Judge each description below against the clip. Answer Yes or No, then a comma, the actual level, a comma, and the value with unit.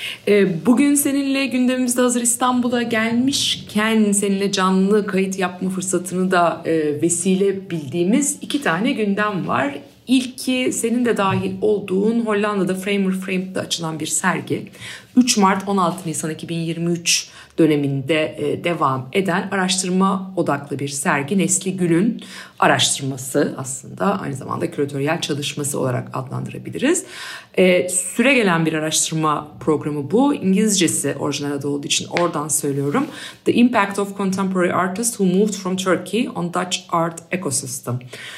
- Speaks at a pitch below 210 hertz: Yes, medium, 185 Hz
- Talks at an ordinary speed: Yes, average, 125 wpm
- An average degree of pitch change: Yes, average, 4.6 semitones